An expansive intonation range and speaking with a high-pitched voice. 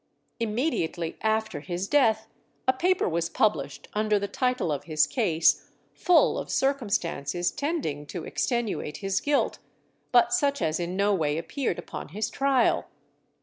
Yes: wide, 7.1 semitones; high, 210 Hz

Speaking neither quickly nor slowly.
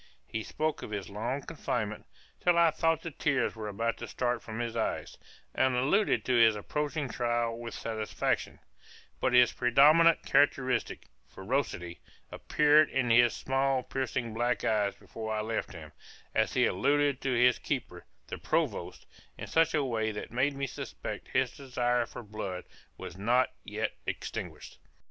Yes: average, 160 wpm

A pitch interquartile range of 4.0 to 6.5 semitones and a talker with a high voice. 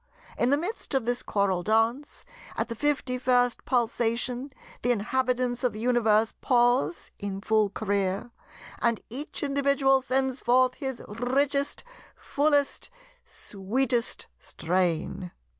No: average, 3.5 semitones; high, 245 Hz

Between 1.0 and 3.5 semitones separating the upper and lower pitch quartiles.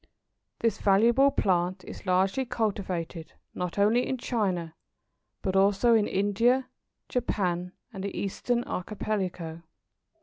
No: average, 4.1 semitones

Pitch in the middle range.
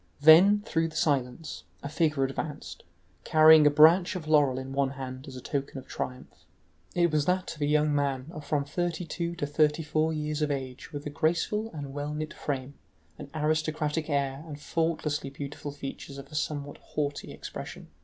Yes: medium, 150 Hz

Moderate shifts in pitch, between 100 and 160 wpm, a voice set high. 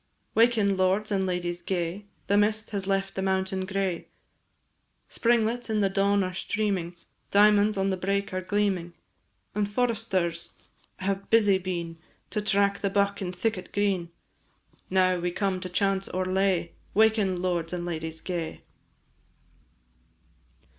No: narrow, 2.0 semitones; average, 140 wpm; high, 195 Hz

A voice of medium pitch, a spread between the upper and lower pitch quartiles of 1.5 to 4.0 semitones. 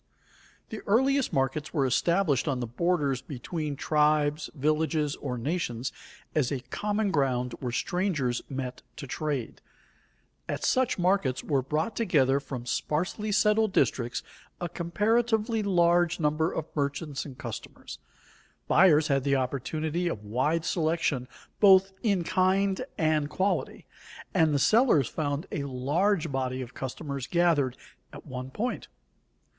No: medium, 155 Hz; wide, 5.4 semitones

